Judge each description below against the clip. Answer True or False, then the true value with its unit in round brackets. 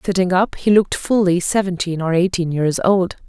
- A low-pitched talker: False (185 Hz)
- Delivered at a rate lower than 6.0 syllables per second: True (5.3 syllables/s)